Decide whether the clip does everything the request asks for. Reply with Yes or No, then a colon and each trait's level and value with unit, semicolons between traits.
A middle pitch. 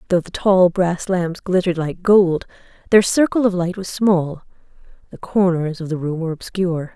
Yes: medium, 180 Hz